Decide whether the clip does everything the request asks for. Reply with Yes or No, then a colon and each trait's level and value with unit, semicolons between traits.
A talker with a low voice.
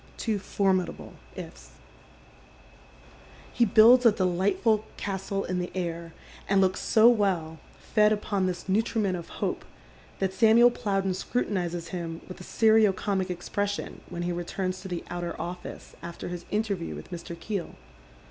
No: high, 190 Hz